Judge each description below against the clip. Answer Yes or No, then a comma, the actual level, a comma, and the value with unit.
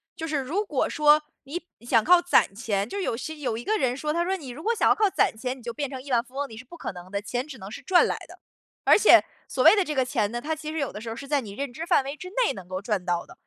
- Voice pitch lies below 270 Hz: No, very high, 275 Hz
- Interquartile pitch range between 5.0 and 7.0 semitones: Yes, wide, 5.4 semitones